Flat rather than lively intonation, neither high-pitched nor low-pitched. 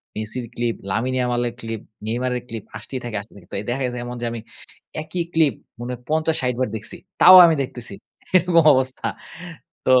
No: narrow, 2.3 semitones; low, 125 Hz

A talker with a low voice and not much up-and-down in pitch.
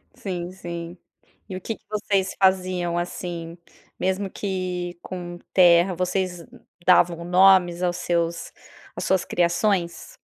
No: medium, 180 Hz; narrow, 1.5 semitones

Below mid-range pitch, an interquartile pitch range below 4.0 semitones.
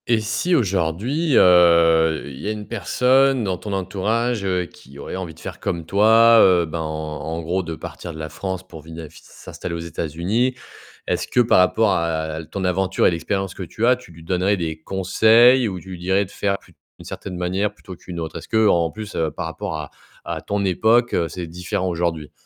No: very low, 90 Hz; average, 4.3 semitones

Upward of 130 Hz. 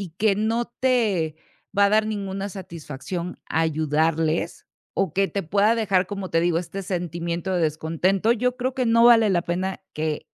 Yes: high, 190 Hz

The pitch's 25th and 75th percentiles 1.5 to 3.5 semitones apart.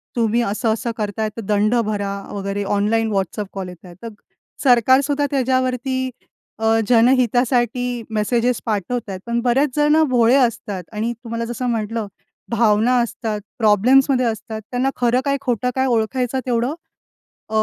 Yes: average, 2.8 semitones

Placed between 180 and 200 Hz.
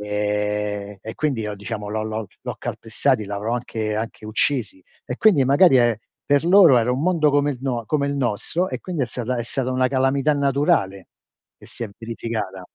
No: low, 120 Hz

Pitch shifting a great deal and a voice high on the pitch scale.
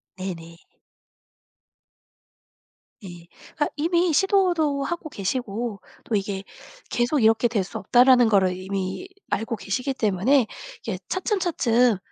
Yes: wide, 6.7 semitones; high, 235 Hz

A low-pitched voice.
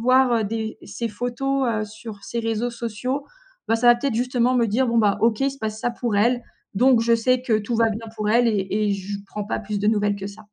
No: high, 230 Hz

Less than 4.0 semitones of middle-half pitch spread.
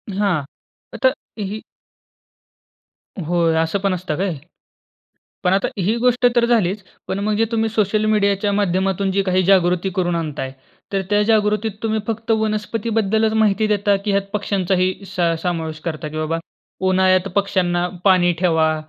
Yes: average, 3.1 semitones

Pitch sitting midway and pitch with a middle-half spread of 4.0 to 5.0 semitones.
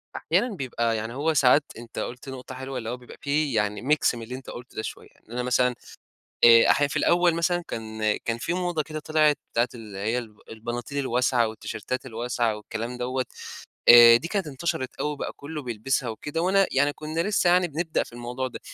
No: low, 130 Hz; average, 4.6 semitones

